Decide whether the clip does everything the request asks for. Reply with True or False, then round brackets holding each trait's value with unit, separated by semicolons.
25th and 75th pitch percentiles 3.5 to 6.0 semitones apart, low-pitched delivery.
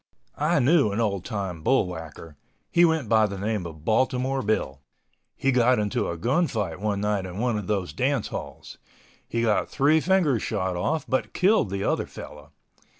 True (5.6 semitones; 110 Hz)